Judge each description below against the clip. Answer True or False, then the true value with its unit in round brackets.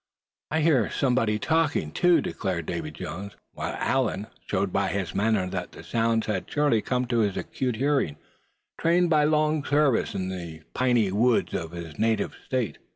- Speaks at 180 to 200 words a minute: False (165 wpm)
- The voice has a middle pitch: False (115 Hz)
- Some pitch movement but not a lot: False (6.6 semitones)